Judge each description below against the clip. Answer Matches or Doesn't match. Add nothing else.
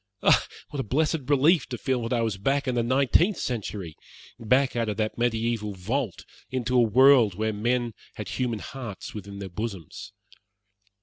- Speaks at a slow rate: Doesn't match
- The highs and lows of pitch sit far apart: Doesn't match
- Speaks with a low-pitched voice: Matches